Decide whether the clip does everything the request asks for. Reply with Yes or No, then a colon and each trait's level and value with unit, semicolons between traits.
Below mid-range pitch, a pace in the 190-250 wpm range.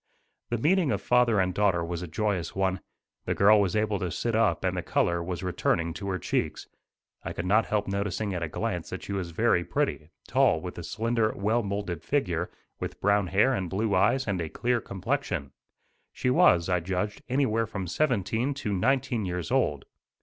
Yes: low, 100 Hz; average, 195 wpm